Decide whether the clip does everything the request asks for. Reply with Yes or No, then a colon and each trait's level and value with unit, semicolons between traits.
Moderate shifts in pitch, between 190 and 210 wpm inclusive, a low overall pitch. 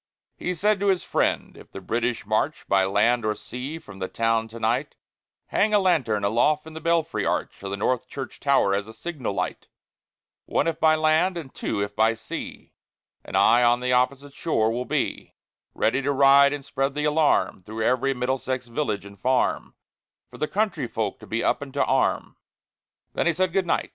No: wide, 5.7 semitones; average, 200 wpm; low, 130 Hz